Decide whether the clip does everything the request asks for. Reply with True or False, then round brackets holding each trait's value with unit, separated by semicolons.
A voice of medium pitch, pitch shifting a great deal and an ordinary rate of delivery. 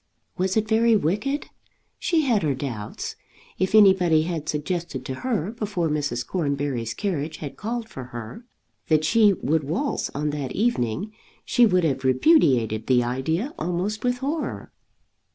True (170 Hz; 7.7 semitones; 150 wpm)